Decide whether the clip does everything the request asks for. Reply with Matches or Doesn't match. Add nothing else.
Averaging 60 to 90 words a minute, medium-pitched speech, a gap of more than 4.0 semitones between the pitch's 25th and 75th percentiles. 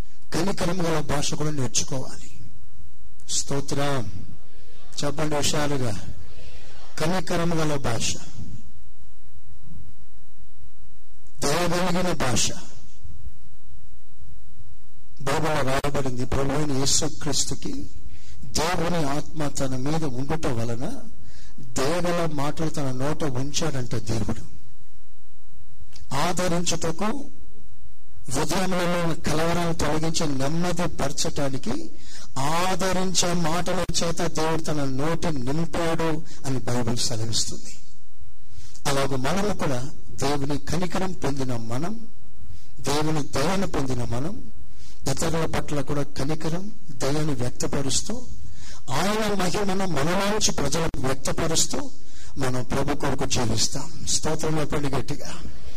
Matches